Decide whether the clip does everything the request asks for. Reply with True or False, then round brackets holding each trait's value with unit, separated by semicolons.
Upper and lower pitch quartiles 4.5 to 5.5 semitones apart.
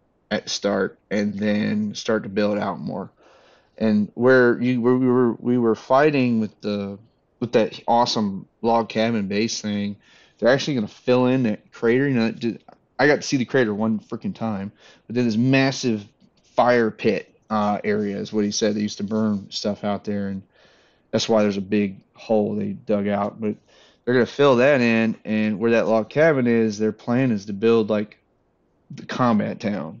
False (2.7 semitones)